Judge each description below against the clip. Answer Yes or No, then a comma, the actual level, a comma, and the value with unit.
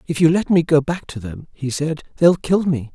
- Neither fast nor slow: No, fast, 265 wpm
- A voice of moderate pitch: Yes, medium, 155 Hz